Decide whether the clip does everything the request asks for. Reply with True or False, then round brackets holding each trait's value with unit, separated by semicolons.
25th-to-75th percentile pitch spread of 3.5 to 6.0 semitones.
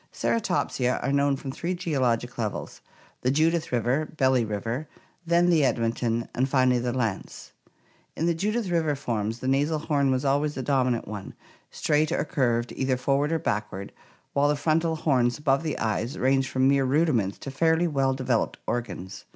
True (4.0 semitones)